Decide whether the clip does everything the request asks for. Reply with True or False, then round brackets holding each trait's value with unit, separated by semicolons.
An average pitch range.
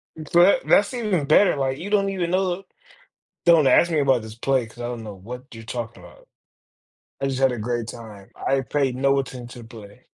False (6.5 semitones)